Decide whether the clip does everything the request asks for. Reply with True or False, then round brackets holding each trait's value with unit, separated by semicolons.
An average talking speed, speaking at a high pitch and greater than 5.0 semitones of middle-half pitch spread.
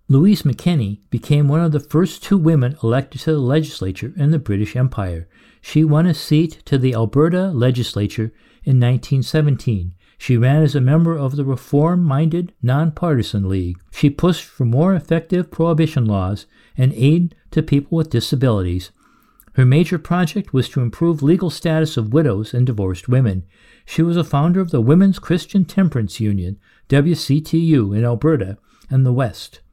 False (160 wpm; 140 Hz; 5.5 semitones)